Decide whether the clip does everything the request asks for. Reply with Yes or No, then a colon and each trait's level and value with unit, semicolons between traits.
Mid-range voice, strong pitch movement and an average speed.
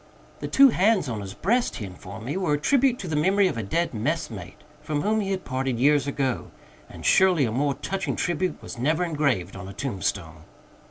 No: medium, 145 Hz; wide, 8.5 semitones; fast, 210 wpm